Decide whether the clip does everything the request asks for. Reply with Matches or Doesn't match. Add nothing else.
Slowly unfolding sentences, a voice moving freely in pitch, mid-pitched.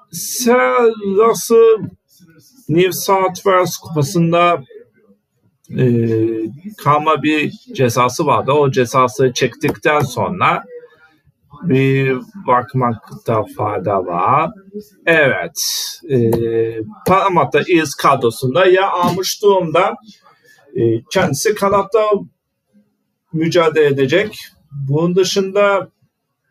Matches